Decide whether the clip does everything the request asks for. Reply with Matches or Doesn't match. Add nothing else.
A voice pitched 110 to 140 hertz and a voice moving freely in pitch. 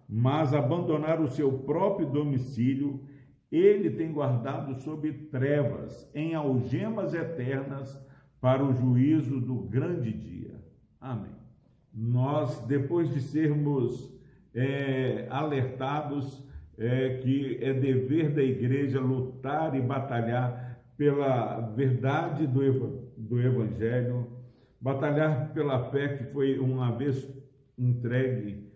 Doesn't match